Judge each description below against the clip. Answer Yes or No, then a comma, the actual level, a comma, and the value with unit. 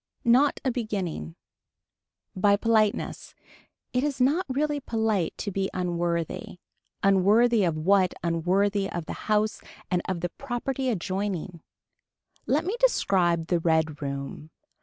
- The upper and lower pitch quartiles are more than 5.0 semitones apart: Yes, wide, 5.5 semitones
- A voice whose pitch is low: No, high, 195 Hz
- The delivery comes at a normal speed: No, slow, 125 wpm